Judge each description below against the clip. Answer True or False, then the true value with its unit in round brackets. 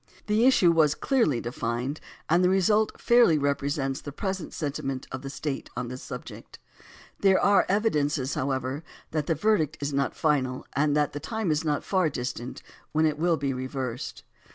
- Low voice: False (150 Hz)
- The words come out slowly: False (175 wpm)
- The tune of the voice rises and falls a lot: False (4.7 semitones)